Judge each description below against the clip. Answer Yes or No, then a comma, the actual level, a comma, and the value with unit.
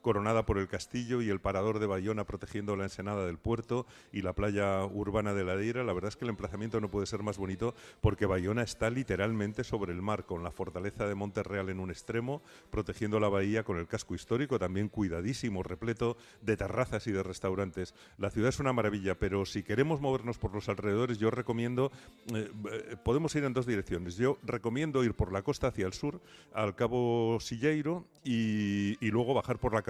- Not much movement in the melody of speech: No, average, 3.2 semitones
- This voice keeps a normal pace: No, fast, 200 wpm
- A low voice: Yes, low, 105 Hz